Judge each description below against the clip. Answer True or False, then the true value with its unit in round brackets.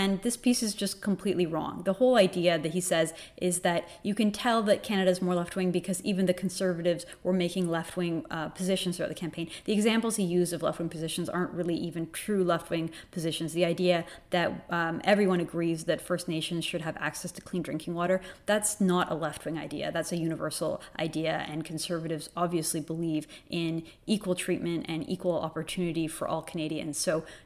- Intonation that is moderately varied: False (2.3 semitones)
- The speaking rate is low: False (190 wpm)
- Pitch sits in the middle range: True (175 Hz)